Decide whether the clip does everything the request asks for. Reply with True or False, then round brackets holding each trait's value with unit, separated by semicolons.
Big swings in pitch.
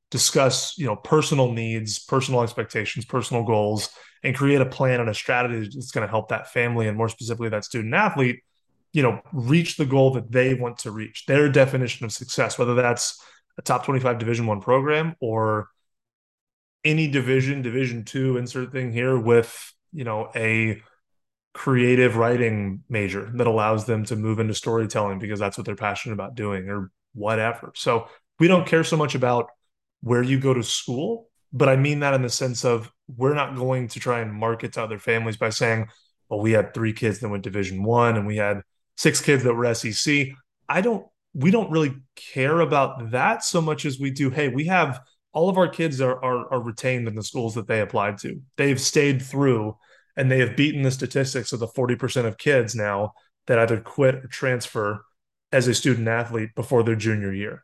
False (3.3 semitones)